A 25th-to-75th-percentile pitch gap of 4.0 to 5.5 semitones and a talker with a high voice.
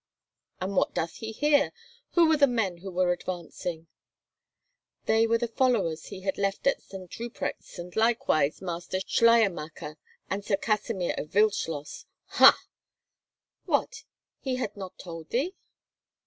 Yes: average, 4.7 semitones; high, 195 Hz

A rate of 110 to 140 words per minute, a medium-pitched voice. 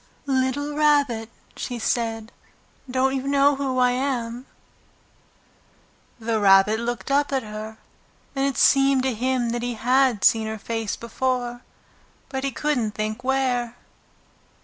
No: slow, 135 wpm; very high, 250 Hz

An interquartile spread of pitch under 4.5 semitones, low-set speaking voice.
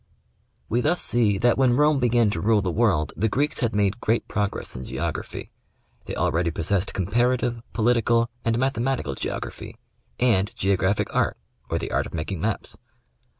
Yes: average, 3.9 semitones; low, 110 Hz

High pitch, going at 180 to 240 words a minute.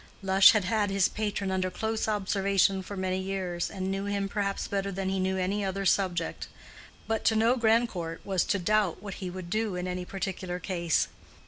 Yes: high, 195 Hz; average, 195 wpm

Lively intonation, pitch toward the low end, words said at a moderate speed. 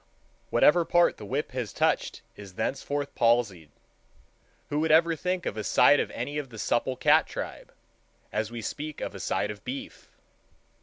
Yes: wide, 5.7 semitones; low, 130 Hz; average, 170 wpm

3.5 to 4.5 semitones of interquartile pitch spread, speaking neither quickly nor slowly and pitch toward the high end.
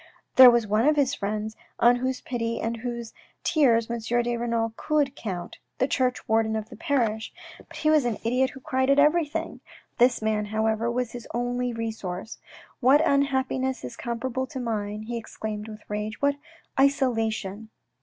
No: average, 3.1 semitones; average, 175 wpm; high, 235 Hz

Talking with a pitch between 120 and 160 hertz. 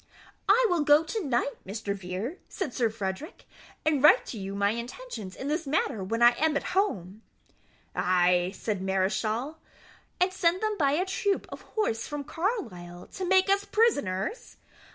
No: very high, 275 Hz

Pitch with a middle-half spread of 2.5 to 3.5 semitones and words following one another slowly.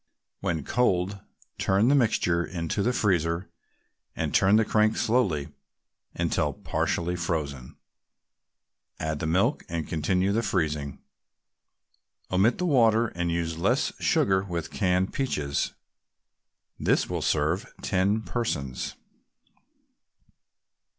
No: average, 4.7 semitones; slow, 110 wpm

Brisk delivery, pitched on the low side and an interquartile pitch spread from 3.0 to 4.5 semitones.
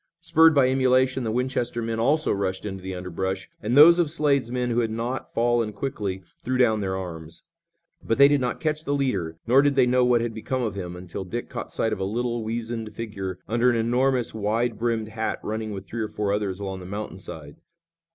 Yes: fast, 220 wpm; low, 115 Hz; average, 4.0 semitones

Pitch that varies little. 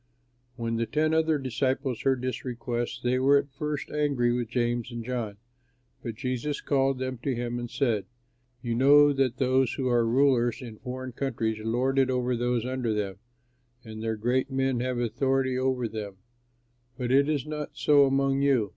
Yes: narrow, 2.3 semitones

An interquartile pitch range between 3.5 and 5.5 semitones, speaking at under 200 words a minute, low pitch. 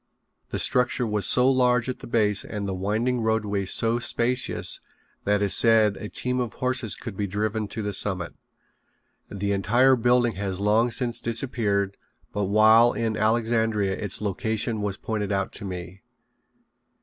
No: average, 2.8 semitones; average, 160 wpm; low, 110 Hz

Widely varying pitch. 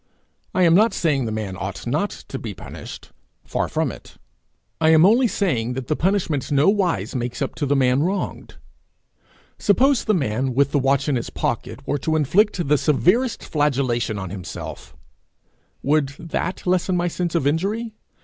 Yes: wide, 5.7 semitones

